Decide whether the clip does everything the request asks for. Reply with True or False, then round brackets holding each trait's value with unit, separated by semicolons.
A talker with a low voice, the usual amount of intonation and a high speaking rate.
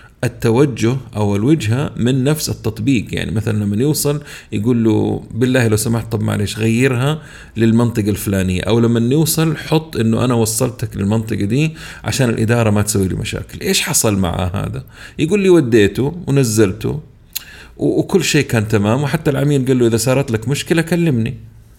True (120 Hz; 4.4 semitones; 155 wpm)